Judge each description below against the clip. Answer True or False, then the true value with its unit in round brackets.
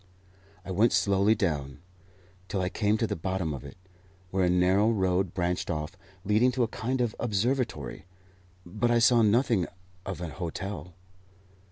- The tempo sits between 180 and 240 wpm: False (160 wpm)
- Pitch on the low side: True (95 Hz)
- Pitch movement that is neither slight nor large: True (4.0 semitones)